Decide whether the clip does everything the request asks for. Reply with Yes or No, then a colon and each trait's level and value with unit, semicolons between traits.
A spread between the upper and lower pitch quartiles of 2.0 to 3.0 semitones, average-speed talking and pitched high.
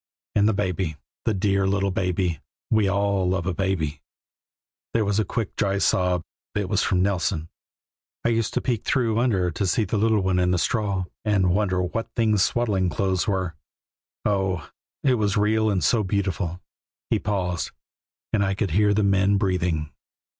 No: narrow, 2.4 semitones; average, 175 wpm; low, 100 Hz